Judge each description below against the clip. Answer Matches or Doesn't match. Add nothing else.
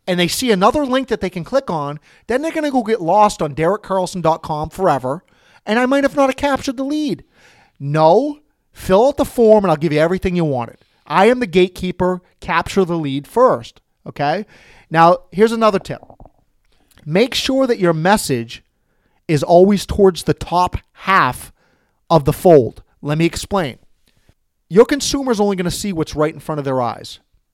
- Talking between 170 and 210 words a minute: Matches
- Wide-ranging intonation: Matches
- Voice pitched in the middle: Matches